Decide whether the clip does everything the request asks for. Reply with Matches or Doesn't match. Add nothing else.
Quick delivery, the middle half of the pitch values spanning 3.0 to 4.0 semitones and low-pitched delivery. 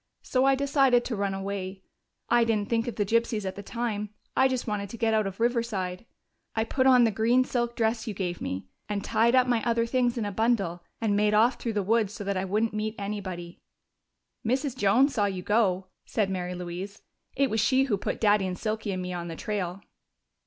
Doesn't match